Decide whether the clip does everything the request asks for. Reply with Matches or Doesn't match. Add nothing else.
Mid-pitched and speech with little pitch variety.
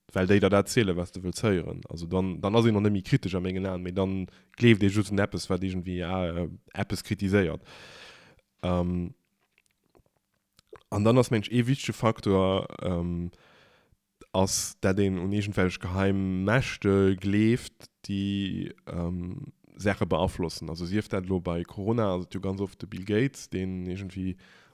Doesn't match